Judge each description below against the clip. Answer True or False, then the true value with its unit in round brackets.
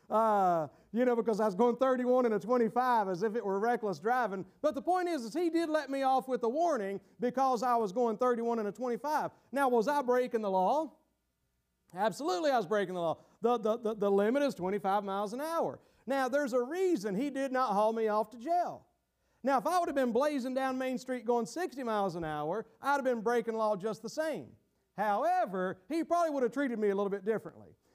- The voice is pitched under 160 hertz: False (240 Hz)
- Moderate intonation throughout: True (4.6 semitones)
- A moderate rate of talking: False (230 wpm)